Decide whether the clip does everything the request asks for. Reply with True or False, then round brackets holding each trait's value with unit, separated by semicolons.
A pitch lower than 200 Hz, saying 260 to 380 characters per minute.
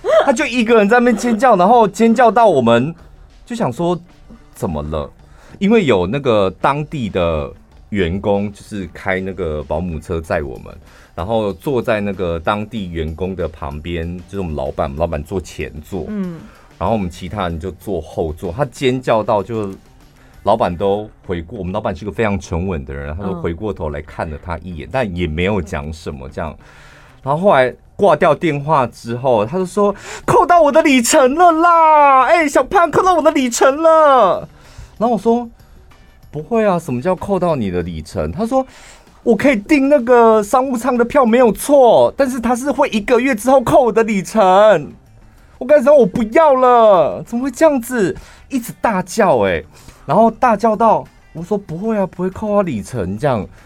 True (185 Hz; 265 characters per minute)